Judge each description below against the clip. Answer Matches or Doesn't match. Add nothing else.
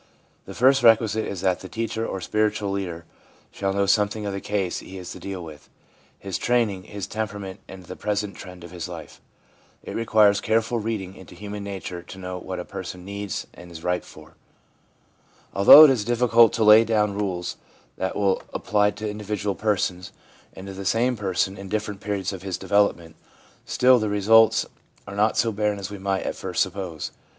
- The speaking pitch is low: Matches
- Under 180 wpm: Doesn't match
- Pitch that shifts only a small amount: Matches